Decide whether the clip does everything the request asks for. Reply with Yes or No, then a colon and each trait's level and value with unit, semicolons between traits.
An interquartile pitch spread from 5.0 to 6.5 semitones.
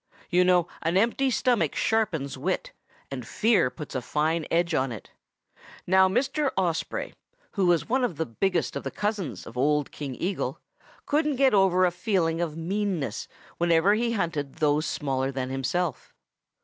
Yes: wide, 5.4 semitones